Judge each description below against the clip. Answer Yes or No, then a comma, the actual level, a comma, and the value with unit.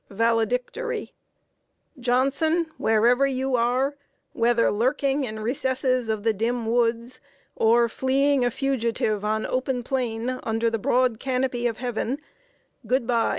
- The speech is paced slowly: Yes, slow, 125 wpm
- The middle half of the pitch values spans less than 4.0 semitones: Yes, narrow, 2.5 semitones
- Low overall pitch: No, high, 245 Hz